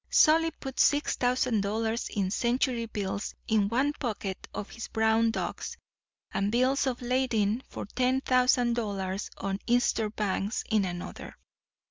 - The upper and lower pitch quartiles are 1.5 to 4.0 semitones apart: Yes, average, 3.6 semitones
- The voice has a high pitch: Yes, high, 230 Hz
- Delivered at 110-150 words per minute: Yes, average, 140 wpm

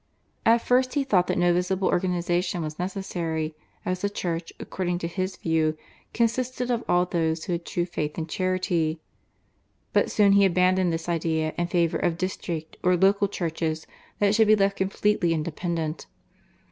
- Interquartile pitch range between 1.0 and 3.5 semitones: Yes, average, 2.8 semitones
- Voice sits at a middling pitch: Yes, medium, 175 Hz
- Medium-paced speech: Yes, average, 165 wpm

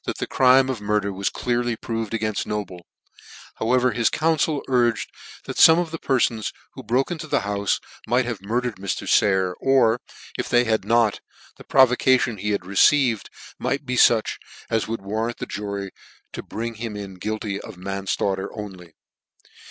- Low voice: Yes, low, 115 Hz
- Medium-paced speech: Yes, average, 165 wpm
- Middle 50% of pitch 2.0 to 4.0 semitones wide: Yes, average, 3.7 semitones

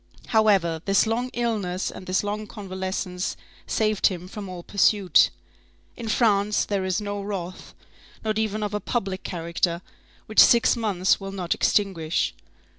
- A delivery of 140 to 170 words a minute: Yes, average, 145 wpm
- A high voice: Yes, high, 200 Hz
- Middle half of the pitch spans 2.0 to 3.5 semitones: Yes, narrow, 2.6 semitones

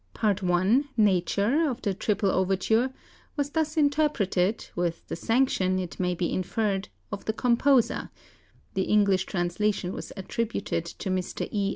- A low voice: No, high, 200 Hz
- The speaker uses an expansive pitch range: No, average, 4.1 semitones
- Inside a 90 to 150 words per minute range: Yes, average, 145 wpm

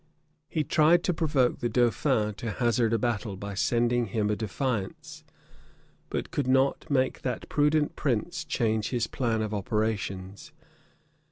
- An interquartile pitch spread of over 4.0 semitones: No, average, 3.7 semitones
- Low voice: Yes, low, 120 Hz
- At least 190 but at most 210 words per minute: No, average, 145 wpm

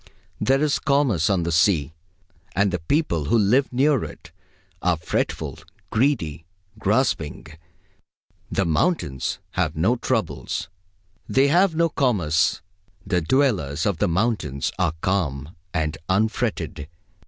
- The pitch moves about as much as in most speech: No, wide, 8.5 semitones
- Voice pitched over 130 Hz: No, very low, 95 Hz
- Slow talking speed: Yes, slow, 120 wpm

